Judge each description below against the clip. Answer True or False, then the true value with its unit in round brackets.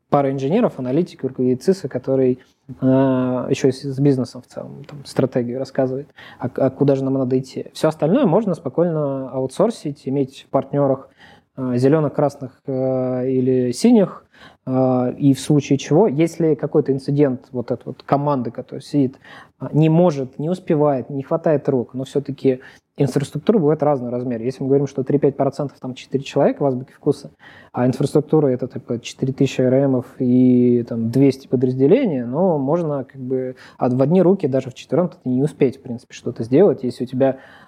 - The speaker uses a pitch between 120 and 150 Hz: True (135 Hz)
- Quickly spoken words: True (165 wpm)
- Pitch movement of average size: False (2.1 semitones)